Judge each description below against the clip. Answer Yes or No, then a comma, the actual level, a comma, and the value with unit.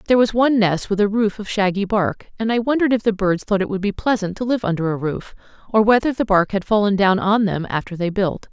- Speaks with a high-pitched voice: Yes, high, 205 Hz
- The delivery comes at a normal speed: No, fast, 270 wpm